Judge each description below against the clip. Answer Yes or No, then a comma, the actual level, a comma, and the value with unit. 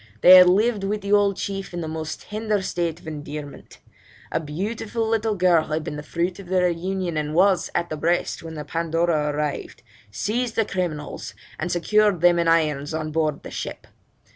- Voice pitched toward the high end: No, medium, 175 Hz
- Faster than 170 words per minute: Yes, average, 190 wpm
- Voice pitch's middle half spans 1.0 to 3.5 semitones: No, average, 4.0 semitones